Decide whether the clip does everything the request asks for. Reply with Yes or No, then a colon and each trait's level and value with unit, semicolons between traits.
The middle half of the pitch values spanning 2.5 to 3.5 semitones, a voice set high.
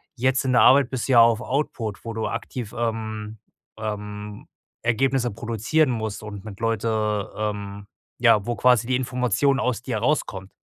No: average, 2.9 semitones; low, 115 Hz